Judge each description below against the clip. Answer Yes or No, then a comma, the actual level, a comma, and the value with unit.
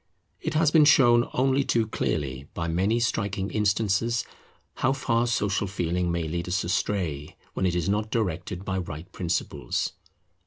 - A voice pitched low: Yes, low, 100 Hz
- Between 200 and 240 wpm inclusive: No, average, 155 wpm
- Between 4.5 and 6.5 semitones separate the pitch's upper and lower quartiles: Yes, average, 5.2 semitones